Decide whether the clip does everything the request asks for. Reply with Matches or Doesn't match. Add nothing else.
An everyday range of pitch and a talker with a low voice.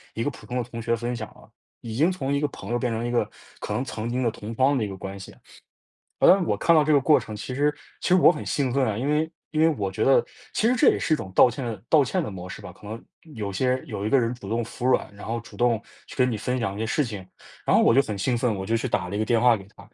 Matches